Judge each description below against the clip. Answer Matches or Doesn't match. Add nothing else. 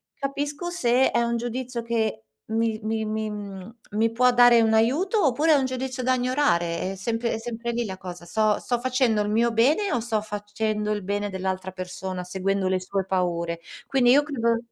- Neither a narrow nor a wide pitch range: Matches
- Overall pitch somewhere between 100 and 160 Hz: Doesn't match